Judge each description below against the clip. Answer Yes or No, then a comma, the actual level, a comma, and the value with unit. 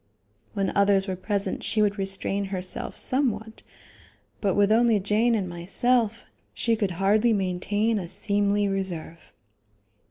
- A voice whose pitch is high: Yes, high, 200 Hz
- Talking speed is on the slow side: Yes, slow, 130 wpm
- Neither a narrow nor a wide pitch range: No, narrow, 2.2 semitones